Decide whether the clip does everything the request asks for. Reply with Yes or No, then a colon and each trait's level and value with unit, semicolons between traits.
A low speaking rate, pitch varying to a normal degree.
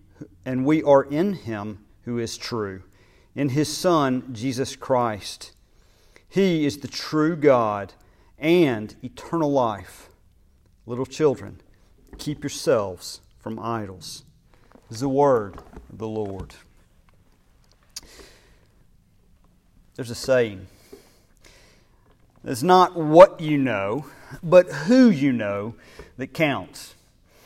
No: slow, 105 wpm; wide, 6.5 semitones